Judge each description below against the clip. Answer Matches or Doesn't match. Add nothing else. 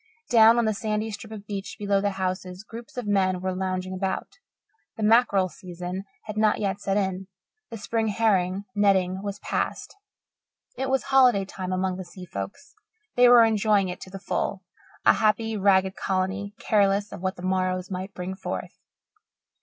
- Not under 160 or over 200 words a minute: Matches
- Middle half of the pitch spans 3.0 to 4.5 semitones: Doesn't match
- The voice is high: Matches